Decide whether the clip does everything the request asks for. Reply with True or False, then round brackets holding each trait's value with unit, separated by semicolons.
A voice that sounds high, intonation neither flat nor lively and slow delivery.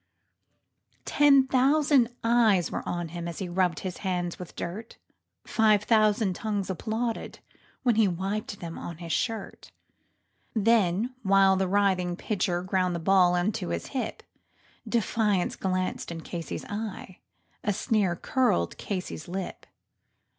True (195 Hz; 3.8 semitones; 130 wpm)